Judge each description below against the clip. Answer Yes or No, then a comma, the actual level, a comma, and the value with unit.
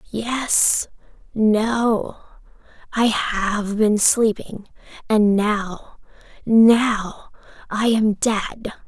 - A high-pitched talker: Yes, high, 215 Hz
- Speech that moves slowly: Yes, slow, 45 wpm